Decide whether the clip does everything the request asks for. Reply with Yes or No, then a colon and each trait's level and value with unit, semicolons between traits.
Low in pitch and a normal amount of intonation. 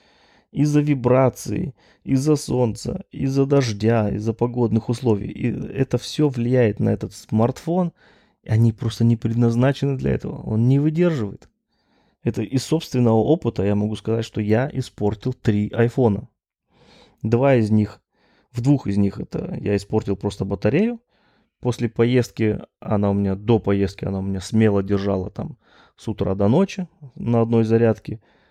Yes: low, 115 Hz; average, 3.8 semitones